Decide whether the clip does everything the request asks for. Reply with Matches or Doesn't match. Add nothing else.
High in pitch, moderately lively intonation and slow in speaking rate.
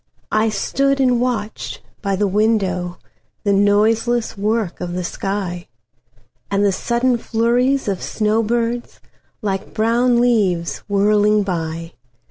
Matches